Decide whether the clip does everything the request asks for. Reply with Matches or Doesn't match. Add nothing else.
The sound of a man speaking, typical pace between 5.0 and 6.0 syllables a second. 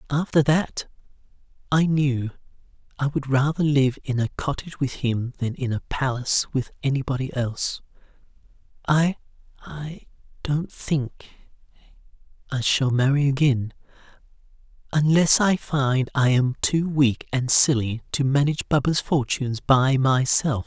Doesn't match